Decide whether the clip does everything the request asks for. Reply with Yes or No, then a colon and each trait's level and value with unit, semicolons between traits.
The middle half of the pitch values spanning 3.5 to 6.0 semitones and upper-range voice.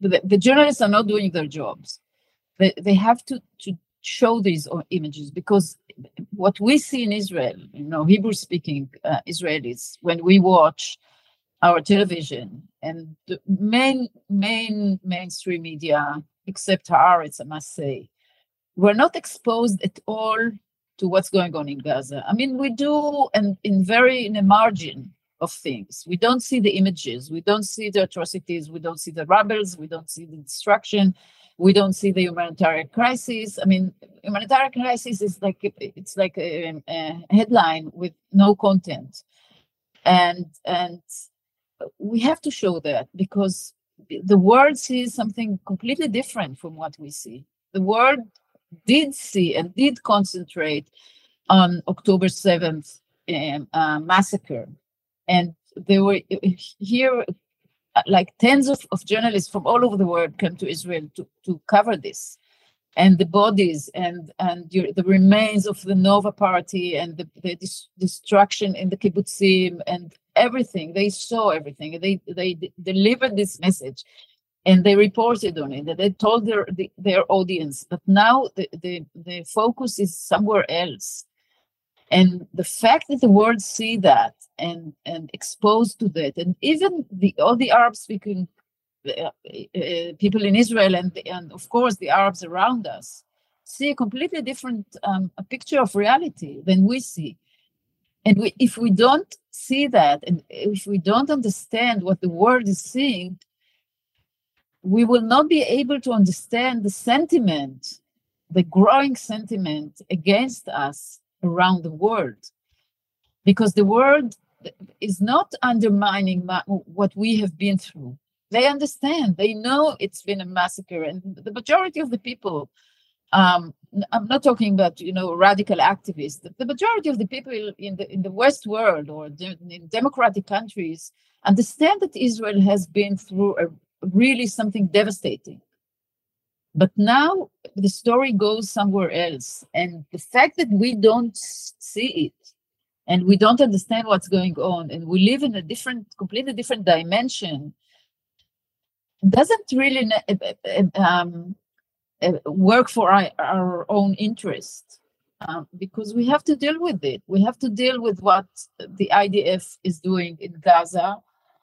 Yes: average, 4.2 semitones; high, 195 Hz